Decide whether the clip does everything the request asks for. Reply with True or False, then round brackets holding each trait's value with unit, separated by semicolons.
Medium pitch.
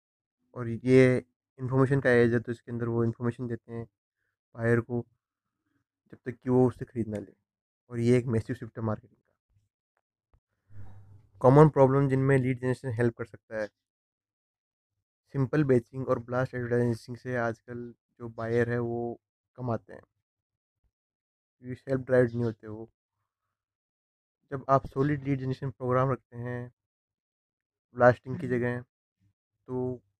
False (120 Hz)